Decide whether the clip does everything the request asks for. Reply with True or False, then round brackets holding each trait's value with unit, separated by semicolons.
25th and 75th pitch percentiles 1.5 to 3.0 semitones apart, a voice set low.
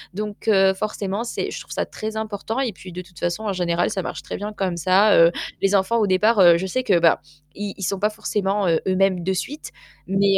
False (2.4 semitones; 195 Hz)